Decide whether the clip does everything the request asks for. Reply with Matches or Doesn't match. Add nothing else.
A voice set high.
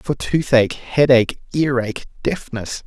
Doesn't match